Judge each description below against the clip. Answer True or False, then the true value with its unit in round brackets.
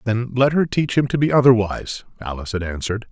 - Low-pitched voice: True (115 Hz)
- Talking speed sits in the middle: False (210 wpm)